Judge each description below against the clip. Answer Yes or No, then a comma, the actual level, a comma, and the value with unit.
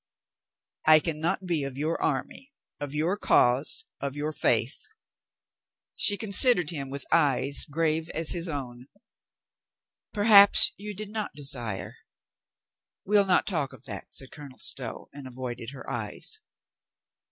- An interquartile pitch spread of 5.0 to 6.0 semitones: Yes, wide, 5.6 semitones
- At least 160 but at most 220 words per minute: No, slow, 135 wpm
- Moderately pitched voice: Yes, medium, 150 Hz